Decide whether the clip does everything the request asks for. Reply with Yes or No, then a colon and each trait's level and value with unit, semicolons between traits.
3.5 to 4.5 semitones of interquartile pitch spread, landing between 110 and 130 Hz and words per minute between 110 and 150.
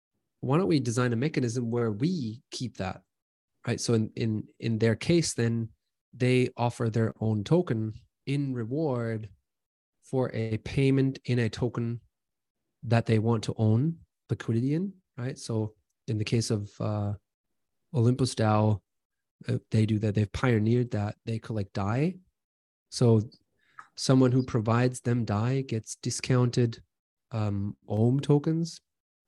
No: average, 2.9 semitones; low, 115 Hz; average, 140 wpm